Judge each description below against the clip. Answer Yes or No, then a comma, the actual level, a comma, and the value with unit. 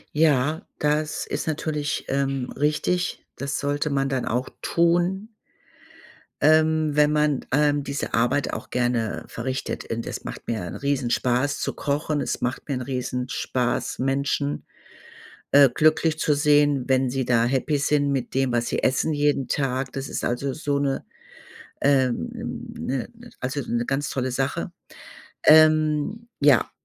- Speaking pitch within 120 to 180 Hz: Yes, medium, 140 Hz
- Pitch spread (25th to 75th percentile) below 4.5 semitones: Yes, average, 2.7 semitones